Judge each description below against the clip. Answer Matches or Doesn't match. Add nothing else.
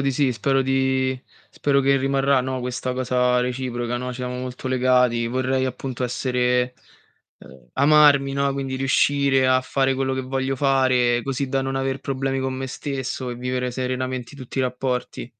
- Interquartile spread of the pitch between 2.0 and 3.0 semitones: Doesn't match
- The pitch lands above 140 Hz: Doesn't match